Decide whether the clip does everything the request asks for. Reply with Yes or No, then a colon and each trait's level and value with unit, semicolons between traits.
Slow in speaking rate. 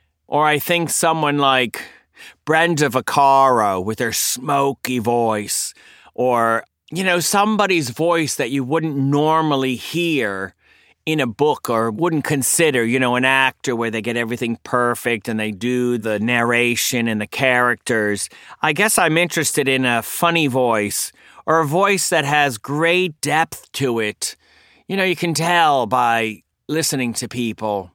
No: average, 150 wpm